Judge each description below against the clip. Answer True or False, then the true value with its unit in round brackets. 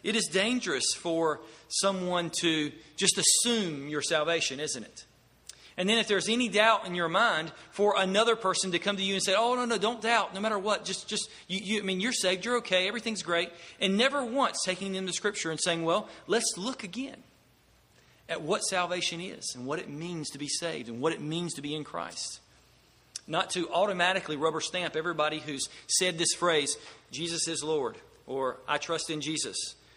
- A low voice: False (180 Hz)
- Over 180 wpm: True (200 wpm)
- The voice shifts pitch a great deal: False (4.5 semitones)